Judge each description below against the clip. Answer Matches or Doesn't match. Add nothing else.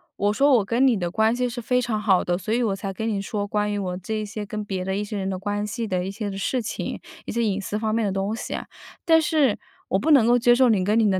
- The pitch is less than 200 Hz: Doesn't match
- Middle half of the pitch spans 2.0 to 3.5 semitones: Matches